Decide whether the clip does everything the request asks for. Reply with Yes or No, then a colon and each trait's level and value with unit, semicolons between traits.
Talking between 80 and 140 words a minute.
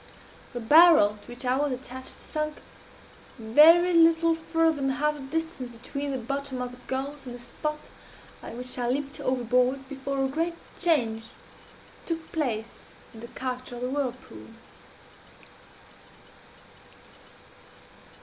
Yes: slow, 135 wpm